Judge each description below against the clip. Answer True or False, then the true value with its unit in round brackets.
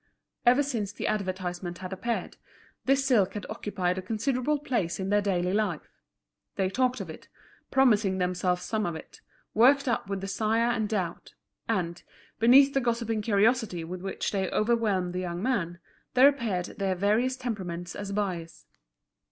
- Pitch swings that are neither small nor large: True (4.5 semitones)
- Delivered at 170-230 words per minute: False (160 wpm)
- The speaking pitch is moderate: False (205 Hz)